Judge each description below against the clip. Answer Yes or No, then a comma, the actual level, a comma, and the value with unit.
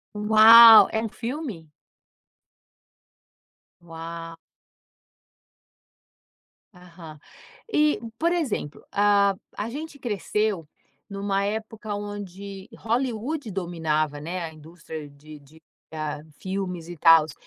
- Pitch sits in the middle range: No, high, 195 Hz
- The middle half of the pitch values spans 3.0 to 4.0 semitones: No, average, 5.1 semitones